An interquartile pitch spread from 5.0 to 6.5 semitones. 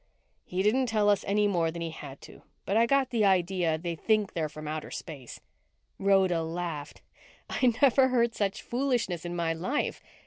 Yes: wide, 5.5 semitones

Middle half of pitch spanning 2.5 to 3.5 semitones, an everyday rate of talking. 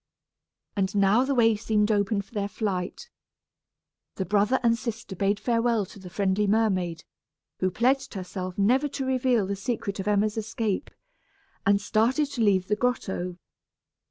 Yes: average, 2.9 semitones; average, 155 wpm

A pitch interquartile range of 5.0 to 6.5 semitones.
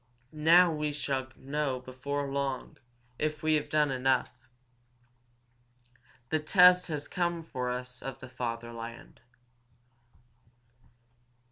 No: average, 3.1 semitones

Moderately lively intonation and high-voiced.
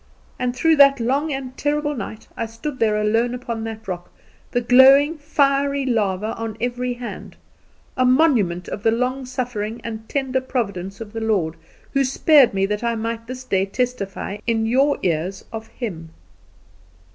Yes: average, 3.5 semitones; high, 235 Hz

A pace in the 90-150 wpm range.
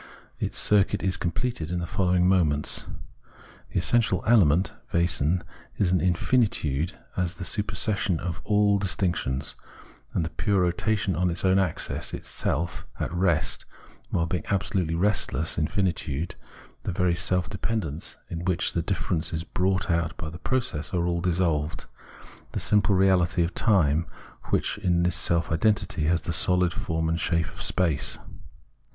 Yes: average, 145 wpm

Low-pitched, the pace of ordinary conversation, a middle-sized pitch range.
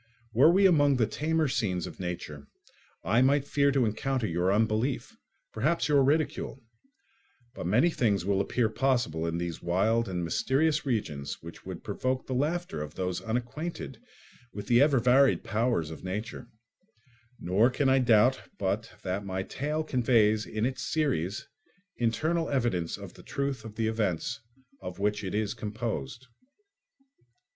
No: low, 115 Hz; average, 150 wpm; wide, 5.9 semitones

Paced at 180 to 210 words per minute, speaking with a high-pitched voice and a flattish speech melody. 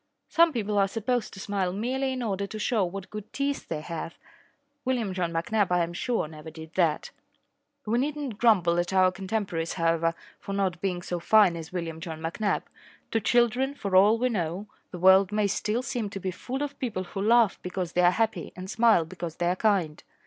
No: fast, 205 wpm; high, 195 Hz; average, 4.4 semitones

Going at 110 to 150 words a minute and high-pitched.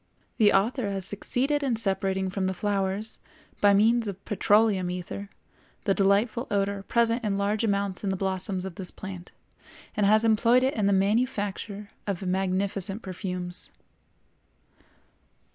Yes: average, 145 wpm; high, 200 Hz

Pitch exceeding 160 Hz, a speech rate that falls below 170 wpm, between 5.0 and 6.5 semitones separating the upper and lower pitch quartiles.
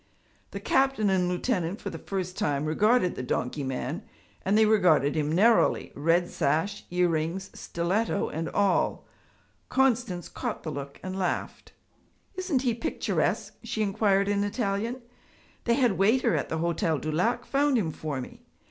Yes: high, 190 Hz; average, 155 wpm; wide, 5.6 semitones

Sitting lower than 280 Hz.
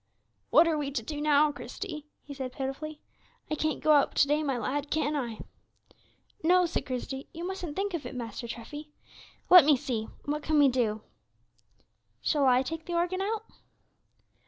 No: very high, 295 Hz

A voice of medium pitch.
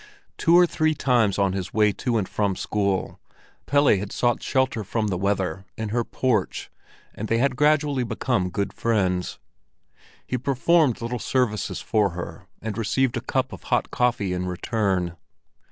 No: low, 110 Hz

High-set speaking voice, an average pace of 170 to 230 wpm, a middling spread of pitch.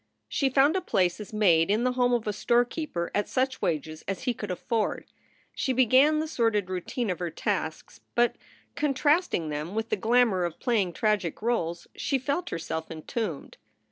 No: high, 220 Hz; average, 180 wpm; wide, 6.5 semitones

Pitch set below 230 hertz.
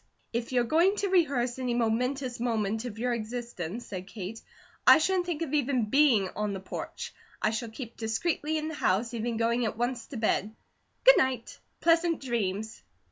No: high, 240 Hz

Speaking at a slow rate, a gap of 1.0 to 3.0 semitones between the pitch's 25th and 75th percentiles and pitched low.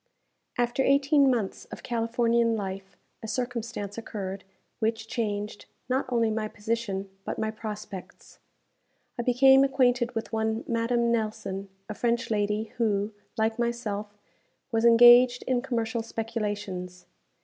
No: slow, 125 wpm; narrow, 2.4 semitones; high, 225 Hz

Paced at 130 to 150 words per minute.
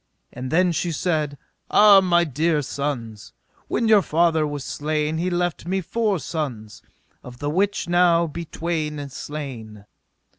Yes: average, 145 wpm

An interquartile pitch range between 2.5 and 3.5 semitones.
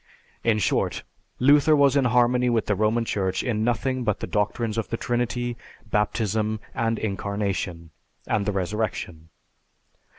Yes: average, 2.8 semitones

